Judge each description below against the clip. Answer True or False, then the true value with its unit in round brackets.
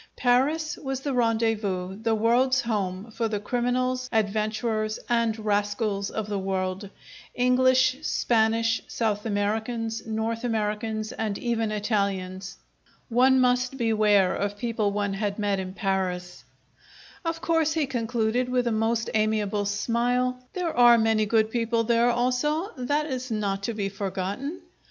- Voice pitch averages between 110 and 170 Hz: False (225 Hz)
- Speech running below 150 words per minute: True (135 wpm)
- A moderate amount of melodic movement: True (3.1 semitones)